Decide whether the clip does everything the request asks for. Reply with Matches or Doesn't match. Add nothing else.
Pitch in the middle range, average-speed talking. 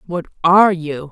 Matches